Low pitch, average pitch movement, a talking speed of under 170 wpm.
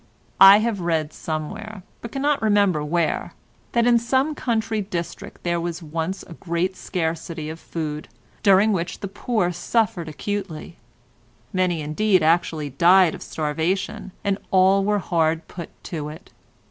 No: medium, 180 Hz; average, 4.2 semitones; average, 145 wpm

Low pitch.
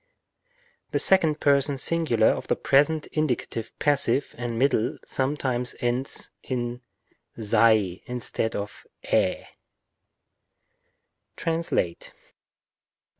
Yes: low, 125 Hz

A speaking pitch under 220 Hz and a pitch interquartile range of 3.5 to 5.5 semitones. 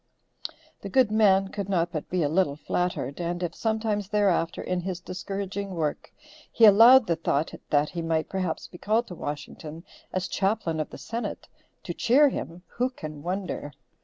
Yes: medium, 185 Hz; average, 4.0 semitones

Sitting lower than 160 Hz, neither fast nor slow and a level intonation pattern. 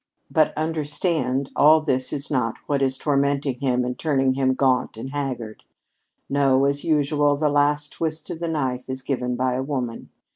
Yes: medium, 140 Hz; average, 175 wpm; narrow, 2.3 semitones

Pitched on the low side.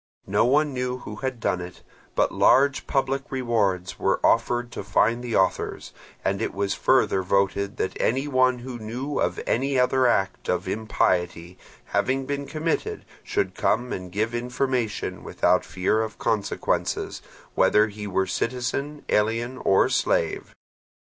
Yes: low, 120 Hz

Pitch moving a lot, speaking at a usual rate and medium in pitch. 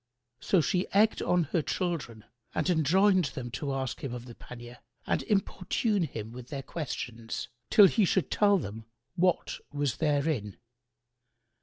Yes: wide, 7.0 semitones; average, 150 wpm; medium, 150 Hz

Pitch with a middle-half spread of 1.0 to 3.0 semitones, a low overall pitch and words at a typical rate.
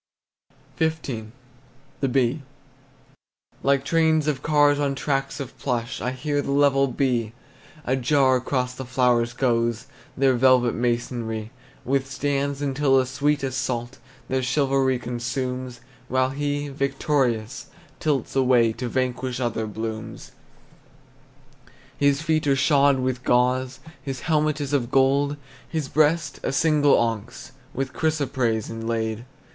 No: narrow, 2.6 semitones; low, 130 Hz; slow, 125 wpm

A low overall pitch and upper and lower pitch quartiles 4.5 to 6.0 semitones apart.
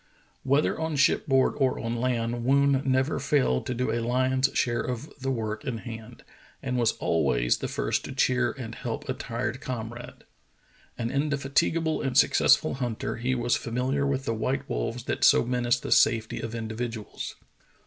No: low, 125 Hz; narrow, 2.6 semitones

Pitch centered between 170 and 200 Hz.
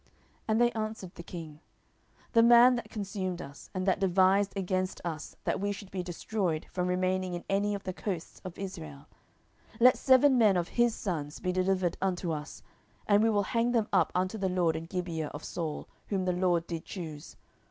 Yes: medium, 185 Hz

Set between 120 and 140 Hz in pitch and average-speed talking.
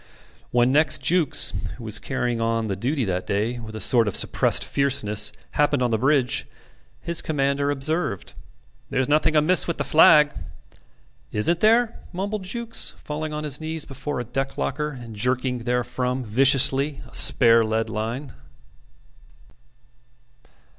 Yes: low, 135 Hz; average, 145 wpm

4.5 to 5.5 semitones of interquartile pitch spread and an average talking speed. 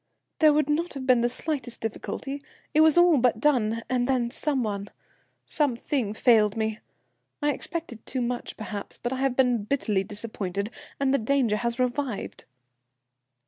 No: average, 4.1 semitones; average, 160 wpm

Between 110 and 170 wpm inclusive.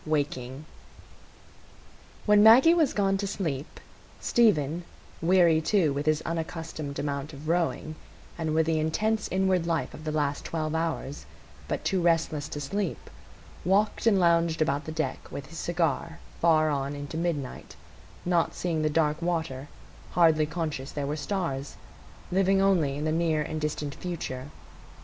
Yes: average, 150 wpm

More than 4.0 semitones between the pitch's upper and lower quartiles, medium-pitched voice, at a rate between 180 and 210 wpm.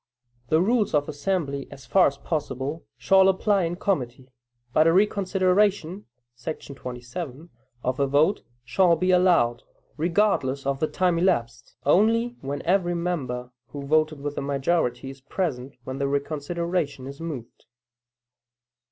No: average, 5.1 semitones; medium, 155 Hz; average, 145 wpm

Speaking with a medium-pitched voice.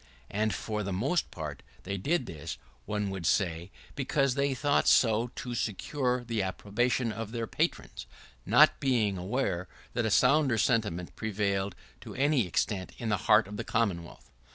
No: low, 110 Hz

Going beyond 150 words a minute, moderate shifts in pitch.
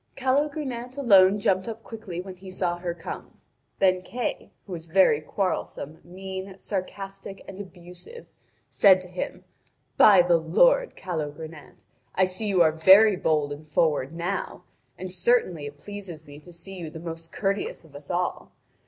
Yes: average, 160 wpm; average, 3.3 semitones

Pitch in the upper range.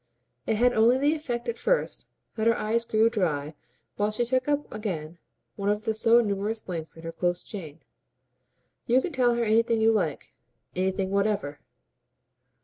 Yes: high, 215 Hz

